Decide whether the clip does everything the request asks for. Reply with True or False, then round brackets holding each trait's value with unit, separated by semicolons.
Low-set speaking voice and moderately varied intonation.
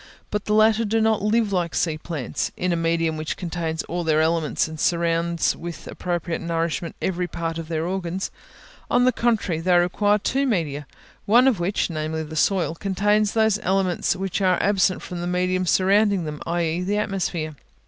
False (175 Hz; 3.5 semitones)